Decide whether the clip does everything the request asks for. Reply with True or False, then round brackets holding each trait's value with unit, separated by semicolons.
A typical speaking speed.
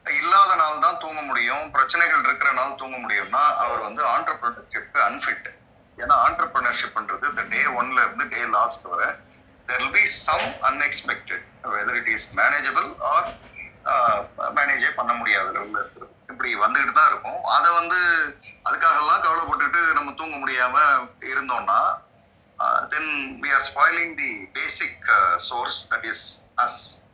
False (65 wpm)